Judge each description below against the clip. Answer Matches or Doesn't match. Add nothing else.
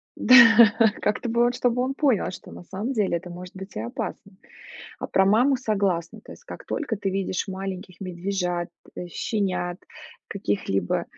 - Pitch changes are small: Doesn't match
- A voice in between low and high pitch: Doesn't match